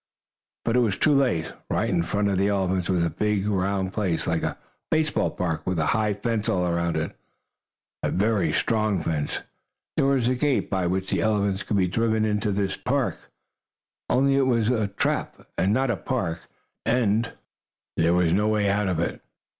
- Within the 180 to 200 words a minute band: Yes, average, 190 wpm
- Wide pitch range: No, average, 3.7 semitones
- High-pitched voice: No, low, 100 Hz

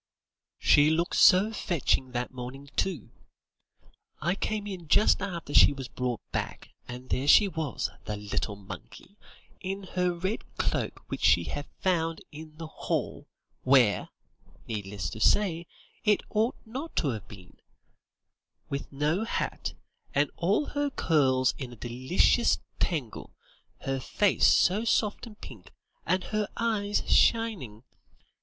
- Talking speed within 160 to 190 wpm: No, slow, 135 wpm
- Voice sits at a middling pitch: Yes, medium, 160 Hz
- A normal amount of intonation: No, wide, 7.8 semitones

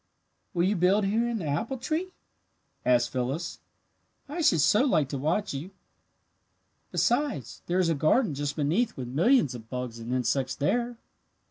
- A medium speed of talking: Yes, average, 160 wpm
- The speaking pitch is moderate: Yes, medium, 165 Hz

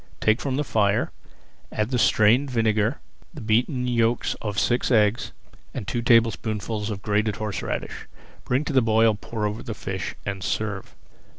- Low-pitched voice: Yes, low, 110 Hz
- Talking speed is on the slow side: No, average, 160 wpm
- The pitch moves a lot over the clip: No, narrow, 2.4 semitones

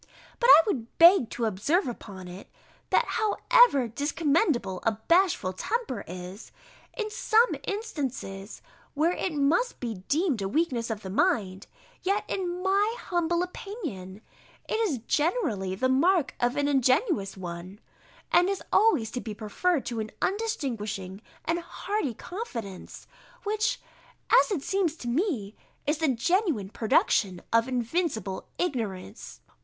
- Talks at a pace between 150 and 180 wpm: No, slow, 135 wpm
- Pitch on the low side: No, very high, 280 Hz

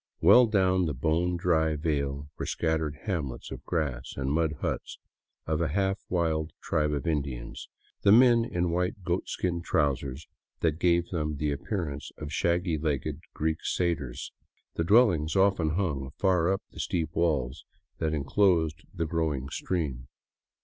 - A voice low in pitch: Yes, very low, 80 Hz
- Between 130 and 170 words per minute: Yes, average, 150 wpm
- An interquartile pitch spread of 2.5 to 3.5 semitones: Yes, average, 3.2 semitones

